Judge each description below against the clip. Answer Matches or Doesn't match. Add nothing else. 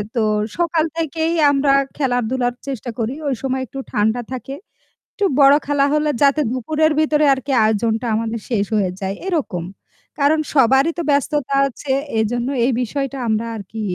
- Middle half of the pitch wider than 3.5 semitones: Matches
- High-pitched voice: Matches